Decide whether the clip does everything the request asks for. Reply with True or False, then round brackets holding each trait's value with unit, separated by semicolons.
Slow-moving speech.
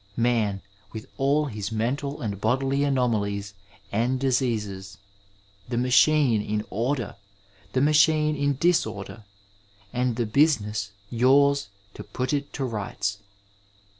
True (120 wpm)